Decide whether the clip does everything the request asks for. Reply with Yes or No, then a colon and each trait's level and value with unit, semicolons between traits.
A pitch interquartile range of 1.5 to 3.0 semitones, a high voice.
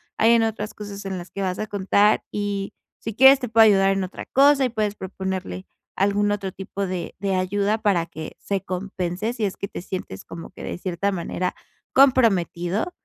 Yes: narrow, 2.5 semitones; high, 200 Hz